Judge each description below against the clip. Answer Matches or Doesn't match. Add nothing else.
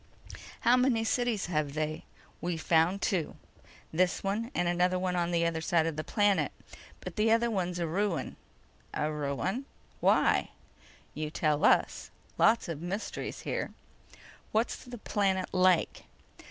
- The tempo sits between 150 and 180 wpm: Doesn't match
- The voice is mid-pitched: Matches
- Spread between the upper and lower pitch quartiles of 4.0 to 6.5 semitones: Matches